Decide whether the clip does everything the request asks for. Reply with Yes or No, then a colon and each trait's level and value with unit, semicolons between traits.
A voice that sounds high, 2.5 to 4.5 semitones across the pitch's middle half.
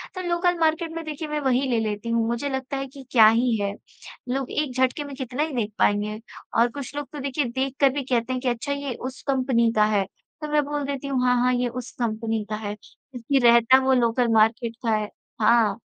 Yes: very high, 250 Hz; average, 3.5 semitones